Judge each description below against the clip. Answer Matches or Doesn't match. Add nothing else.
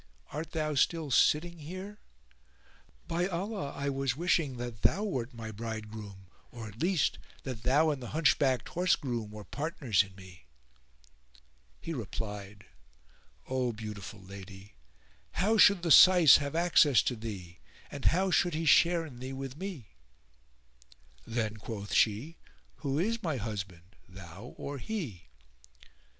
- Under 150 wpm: Matches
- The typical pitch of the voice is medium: Doesn't match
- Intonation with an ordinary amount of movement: Doesn't match